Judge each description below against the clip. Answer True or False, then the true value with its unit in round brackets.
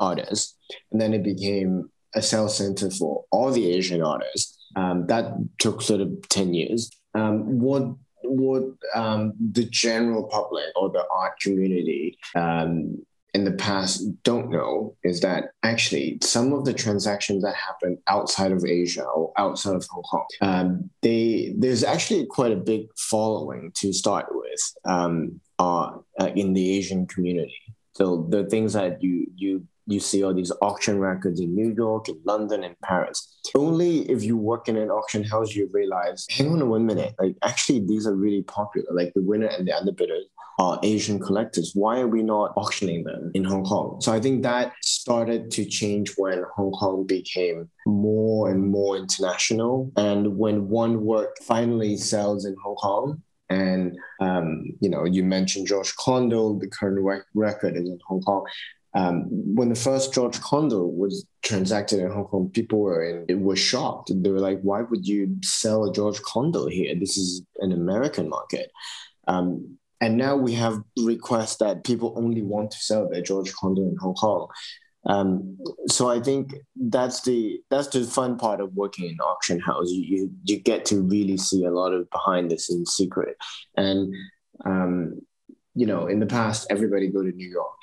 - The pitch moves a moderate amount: True (3.3 semitones)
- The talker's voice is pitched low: True (105 Hz)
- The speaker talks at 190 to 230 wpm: False (180 wpm)